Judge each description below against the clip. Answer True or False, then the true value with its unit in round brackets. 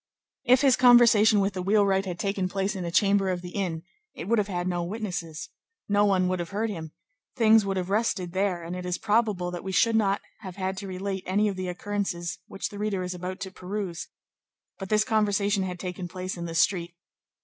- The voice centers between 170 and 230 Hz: True (190 Hz)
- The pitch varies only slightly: True (2.3 semitones)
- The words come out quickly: True (220 wpm)